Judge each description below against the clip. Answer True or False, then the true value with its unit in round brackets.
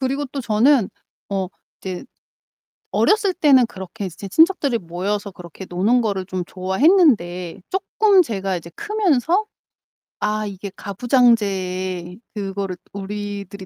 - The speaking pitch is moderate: False (205 Hz)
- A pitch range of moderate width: False (5.8 semitones)